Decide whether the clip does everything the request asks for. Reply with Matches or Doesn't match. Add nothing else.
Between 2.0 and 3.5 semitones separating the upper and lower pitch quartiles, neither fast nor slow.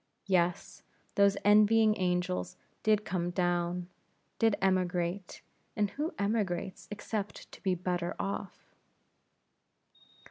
Doesn't match